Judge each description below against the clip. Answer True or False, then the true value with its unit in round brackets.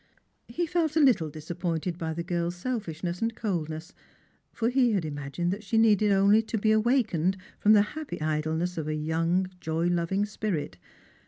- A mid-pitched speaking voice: True (180 Hz)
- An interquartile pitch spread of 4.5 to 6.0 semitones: True (5.2 semitones)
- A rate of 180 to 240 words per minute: False (170 wpm)